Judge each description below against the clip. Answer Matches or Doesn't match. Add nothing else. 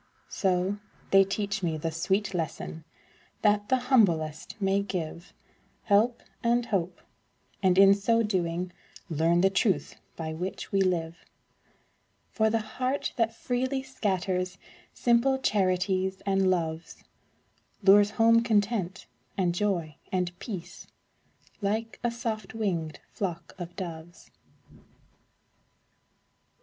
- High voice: Matches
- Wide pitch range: Doesn't match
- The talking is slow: Matches